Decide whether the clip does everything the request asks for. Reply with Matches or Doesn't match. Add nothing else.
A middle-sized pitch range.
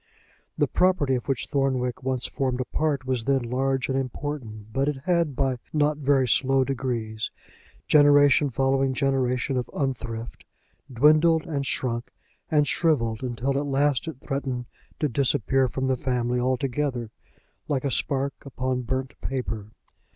Doesn't match